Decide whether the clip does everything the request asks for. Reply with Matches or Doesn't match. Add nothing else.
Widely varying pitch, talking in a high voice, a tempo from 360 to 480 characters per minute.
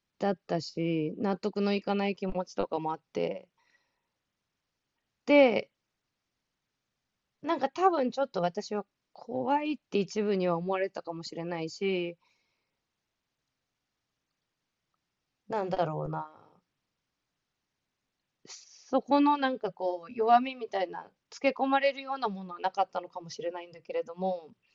Doesn't match